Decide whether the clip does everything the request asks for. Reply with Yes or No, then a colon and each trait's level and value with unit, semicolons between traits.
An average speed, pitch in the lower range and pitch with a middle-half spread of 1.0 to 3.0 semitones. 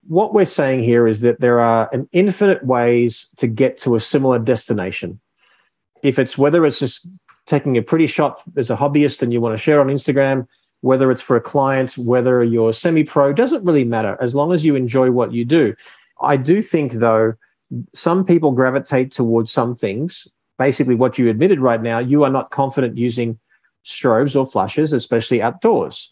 No: average, 185 wpm; low, 130 Hz; average, 3.6 semitones